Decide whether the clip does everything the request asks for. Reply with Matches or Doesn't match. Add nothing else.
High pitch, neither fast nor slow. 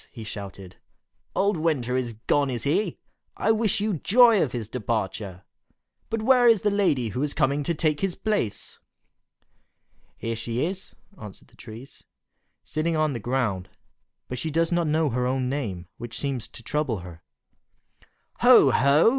Doesn't match